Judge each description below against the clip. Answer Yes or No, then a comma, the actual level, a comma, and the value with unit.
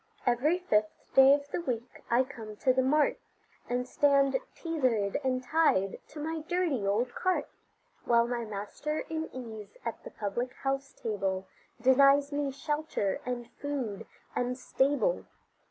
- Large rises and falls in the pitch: No, average, 3.8 semitones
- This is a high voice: Yes, very high, 260 Hz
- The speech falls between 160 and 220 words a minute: No, average, 145 wpm